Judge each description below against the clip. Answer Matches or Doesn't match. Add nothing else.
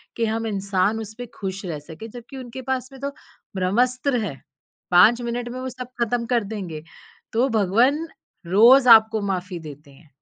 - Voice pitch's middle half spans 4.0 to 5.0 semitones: Matches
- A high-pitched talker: Matches